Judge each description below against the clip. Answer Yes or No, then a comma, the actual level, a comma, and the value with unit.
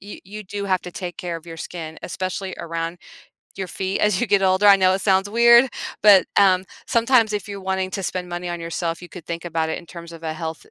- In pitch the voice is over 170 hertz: Yes, medium, 185 Hz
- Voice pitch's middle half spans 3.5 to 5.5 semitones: No, average, 2.8 semitones